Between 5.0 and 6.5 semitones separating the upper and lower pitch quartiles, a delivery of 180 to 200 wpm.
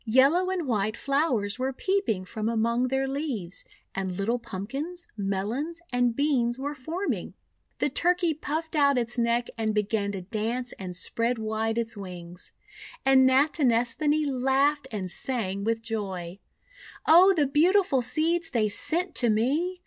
No: wide, 5.4 semitones; average, 150 wpm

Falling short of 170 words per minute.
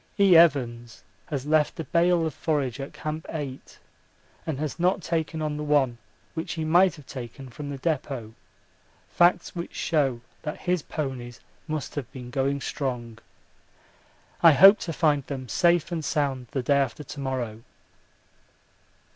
Yes: average, 155 wpm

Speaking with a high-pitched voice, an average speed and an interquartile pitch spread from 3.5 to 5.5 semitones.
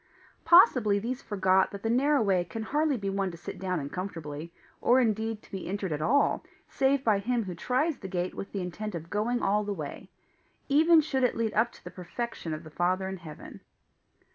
No: high, 205 Hz; fast, 215 wpm; average, 5.1 semitones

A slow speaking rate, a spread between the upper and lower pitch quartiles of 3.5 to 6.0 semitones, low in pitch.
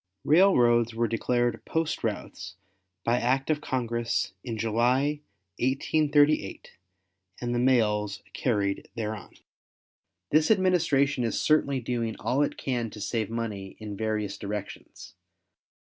Yes: slow, 120 wpm; average, 4.1 semitones; low, 120 Hz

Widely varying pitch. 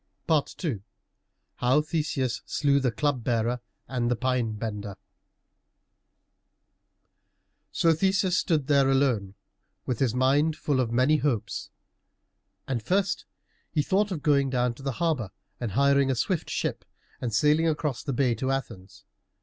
No: average, 4.0 semitones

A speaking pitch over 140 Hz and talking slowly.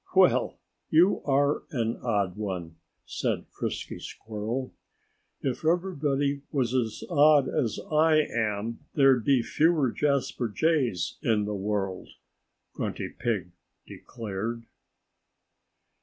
No: low, 120 Hz; slow, 105 wpm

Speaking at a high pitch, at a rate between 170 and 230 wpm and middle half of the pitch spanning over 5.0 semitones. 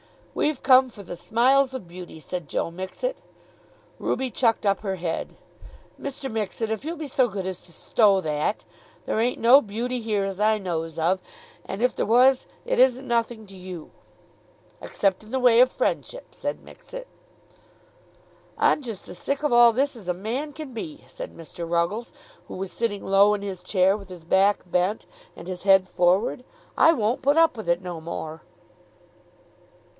Yes: high, 215 Hz; average, 180 wpm; wide, 5.6 semitones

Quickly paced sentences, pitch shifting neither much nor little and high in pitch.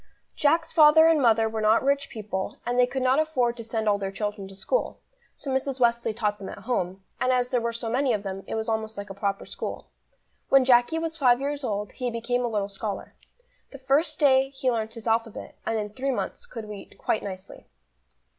Yes: fast, 220 wpm; average, 4.0 semitones; high, 235 Hz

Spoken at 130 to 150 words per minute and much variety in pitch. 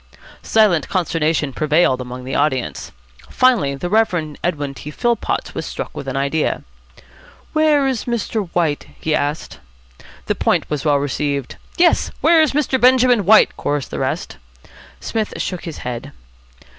Yes: average, 145 wpm; wide, 7.9 semitones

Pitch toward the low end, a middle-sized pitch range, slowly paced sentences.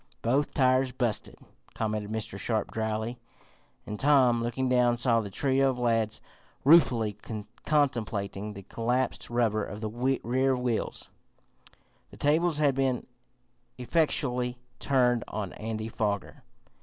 Yes: low, 120 Hz; average, 3.2 semitones; slow, 120 wpm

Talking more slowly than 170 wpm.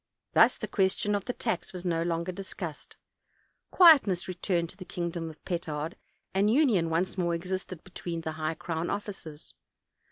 Yes: average, 160 wpm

